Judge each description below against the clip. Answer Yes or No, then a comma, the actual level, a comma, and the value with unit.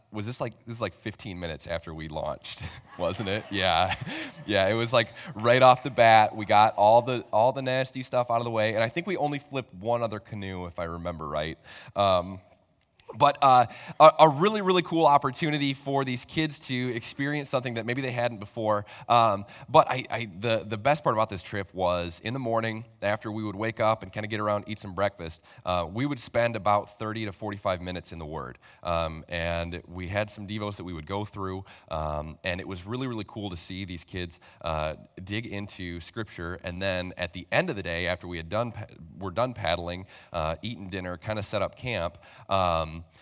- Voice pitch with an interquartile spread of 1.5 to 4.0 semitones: No, average, 4.8 semitones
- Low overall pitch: Yes, low, 105 Hz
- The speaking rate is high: Yes, fast, 215 wpm